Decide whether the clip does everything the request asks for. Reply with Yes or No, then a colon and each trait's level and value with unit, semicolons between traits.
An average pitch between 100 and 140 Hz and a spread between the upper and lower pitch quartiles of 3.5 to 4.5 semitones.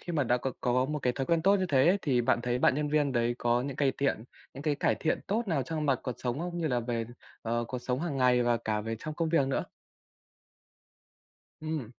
Yes: low, 135 Hz; average, 4.1 semitones